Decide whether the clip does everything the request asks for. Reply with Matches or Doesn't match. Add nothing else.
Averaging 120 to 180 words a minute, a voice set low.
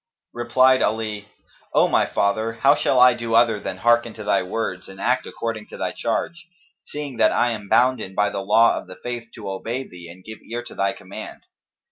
Doesn't match